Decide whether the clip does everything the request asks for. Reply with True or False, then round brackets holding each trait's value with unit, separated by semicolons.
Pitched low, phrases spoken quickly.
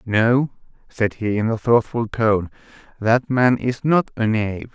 False (115 Hz; 165 wpm)